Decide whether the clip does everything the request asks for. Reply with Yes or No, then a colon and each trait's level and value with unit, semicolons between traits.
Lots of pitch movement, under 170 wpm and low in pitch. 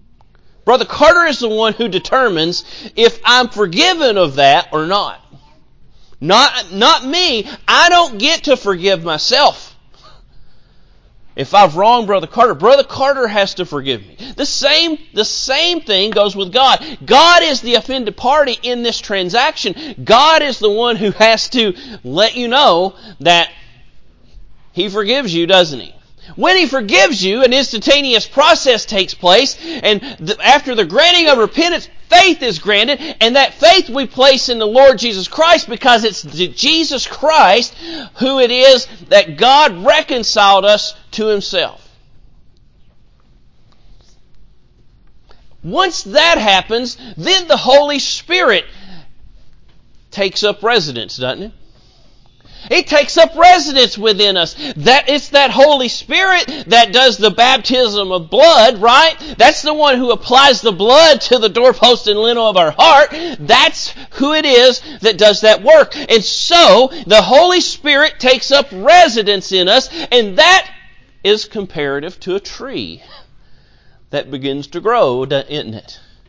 No: wide, 6.2 semitones; average, 145 wpm; very high, 250 Hz